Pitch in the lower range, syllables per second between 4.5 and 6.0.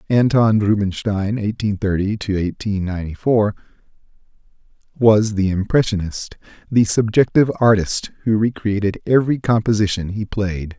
No: low, 105 Hz; 4.0 syllables/s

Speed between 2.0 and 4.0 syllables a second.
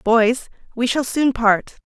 Yes: 3.6 syllables/s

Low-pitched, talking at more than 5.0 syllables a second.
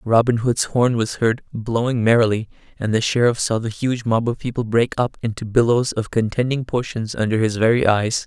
Yes: low, 115 Hz; 5.2 syllables/s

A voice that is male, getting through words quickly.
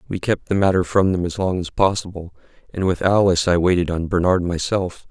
Yes: male; fast, 210 wpm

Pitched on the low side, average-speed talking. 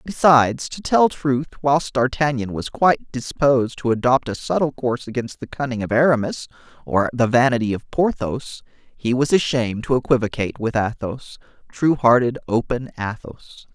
Yes: low, 125 Hz; average, 155 wpm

